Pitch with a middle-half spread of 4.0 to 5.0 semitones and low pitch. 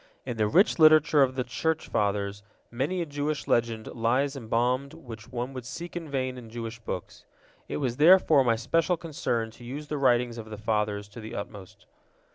Yes: average, 4.5 semitones; low, 125 Hz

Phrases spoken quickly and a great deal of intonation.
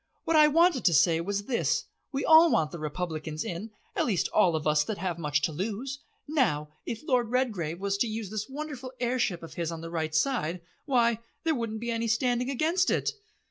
Yes: fast, 215 wpm; wide, 7.5 semitones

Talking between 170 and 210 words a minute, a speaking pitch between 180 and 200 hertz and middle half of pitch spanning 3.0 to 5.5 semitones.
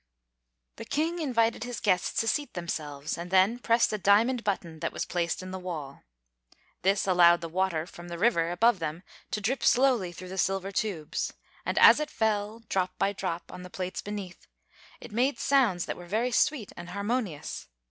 Yes: average, 190 wpm; high, 190 Hz; average, 4.7 semitones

